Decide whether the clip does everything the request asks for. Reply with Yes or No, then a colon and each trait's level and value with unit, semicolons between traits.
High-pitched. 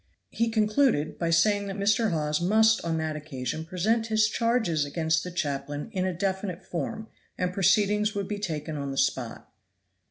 No: medium, 180 Hz